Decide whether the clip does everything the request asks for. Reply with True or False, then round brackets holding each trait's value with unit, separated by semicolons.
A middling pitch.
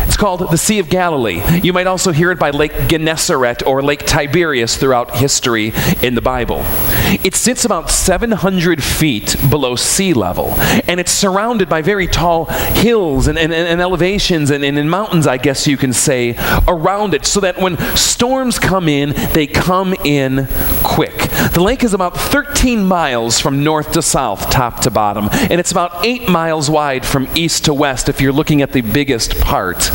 True (160 Hz)